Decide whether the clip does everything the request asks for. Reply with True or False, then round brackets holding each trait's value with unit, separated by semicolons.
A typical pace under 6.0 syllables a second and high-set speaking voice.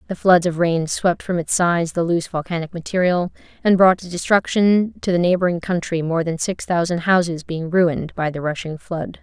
False (5.2 syllables/s; 175 Hz)